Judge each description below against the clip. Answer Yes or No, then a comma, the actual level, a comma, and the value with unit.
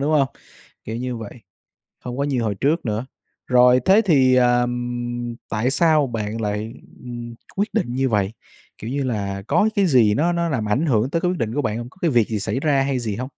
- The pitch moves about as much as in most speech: Yes, average, 4.0 semitones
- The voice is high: No, low, 125 Hz